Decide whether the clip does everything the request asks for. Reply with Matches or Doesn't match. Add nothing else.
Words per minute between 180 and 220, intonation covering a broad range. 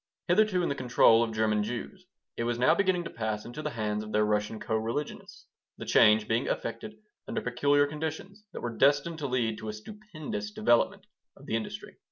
Matches